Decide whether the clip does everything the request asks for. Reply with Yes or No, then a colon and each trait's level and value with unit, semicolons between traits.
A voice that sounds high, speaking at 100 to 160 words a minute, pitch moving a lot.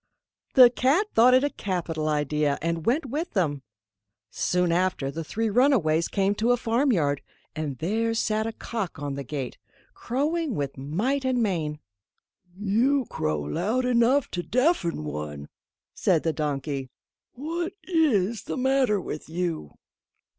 Yes: high, 195 Hz; average, 145 wpm; wide, 8.8 semitones